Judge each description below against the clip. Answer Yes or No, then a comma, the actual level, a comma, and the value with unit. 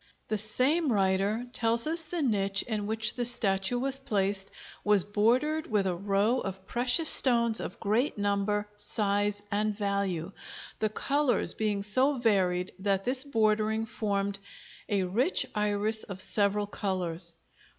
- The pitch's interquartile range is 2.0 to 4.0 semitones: Yes, average, 3.1 semitones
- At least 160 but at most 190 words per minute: No, average, 140 wpm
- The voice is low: No, high, 210 Hz